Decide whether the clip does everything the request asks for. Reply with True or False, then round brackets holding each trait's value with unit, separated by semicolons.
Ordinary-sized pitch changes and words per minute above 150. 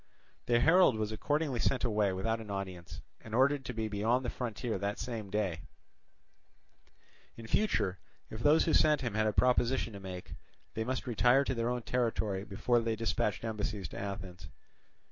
True (3.5 semitones; 175 wpm)